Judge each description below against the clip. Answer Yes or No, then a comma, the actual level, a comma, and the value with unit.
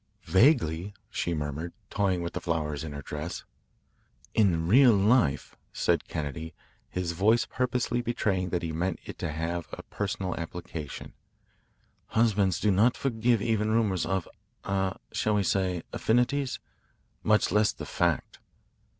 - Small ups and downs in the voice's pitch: No, average, 4.7 semitones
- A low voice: Yes, very low, 95 Hz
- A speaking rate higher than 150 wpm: No, average, 140 wpm